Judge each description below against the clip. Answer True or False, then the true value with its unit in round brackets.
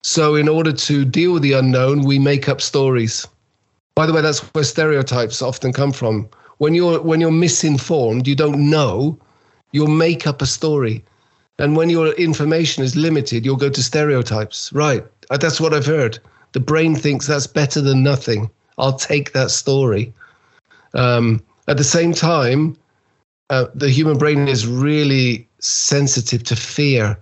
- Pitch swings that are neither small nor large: True (3.4 semitones)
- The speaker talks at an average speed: False (165 wpm)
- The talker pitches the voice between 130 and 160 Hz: True (140 Hz)